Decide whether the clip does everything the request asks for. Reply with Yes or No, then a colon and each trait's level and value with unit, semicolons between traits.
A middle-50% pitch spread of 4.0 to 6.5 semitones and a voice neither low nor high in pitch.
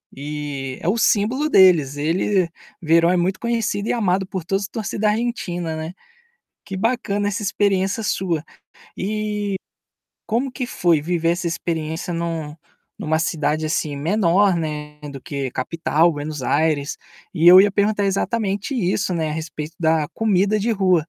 Yes: average, 4.4 semitones; medium, 180 Hz